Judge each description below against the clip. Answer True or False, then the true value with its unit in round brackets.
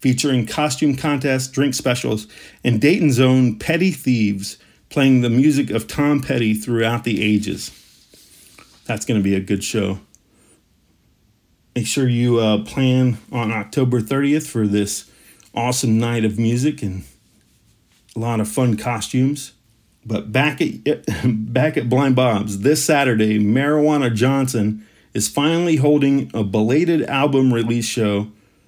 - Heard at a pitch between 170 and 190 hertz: False (120 Hz)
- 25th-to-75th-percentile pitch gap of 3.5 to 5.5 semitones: True (4.2 semitones)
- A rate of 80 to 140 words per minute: True (135 wpm)